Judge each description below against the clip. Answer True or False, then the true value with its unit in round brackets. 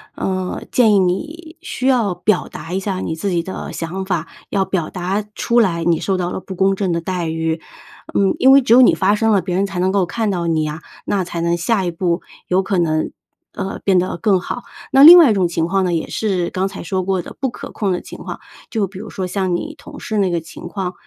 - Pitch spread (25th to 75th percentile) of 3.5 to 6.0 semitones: False (2.8 semitones)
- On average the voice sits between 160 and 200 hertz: True (190 Hz)